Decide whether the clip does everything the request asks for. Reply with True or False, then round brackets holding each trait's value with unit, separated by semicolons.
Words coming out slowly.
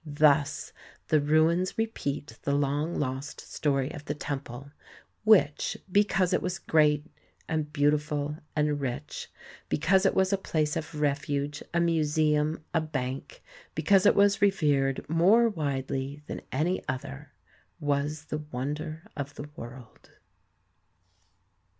True (125 wpm)